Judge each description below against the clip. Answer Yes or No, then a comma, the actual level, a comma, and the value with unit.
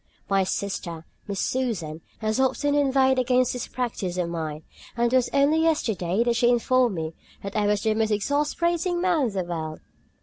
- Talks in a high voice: Yes, high, 235 Hz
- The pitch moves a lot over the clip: Yes, wide, 5.9 semitones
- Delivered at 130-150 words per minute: No, average, 180 wpm